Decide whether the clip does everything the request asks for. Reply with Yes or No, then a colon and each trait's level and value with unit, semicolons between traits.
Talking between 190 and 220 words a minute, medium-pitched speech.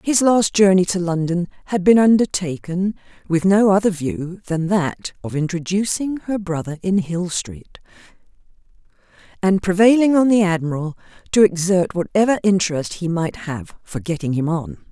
No: average, 150 wpm; medium, 180 Hz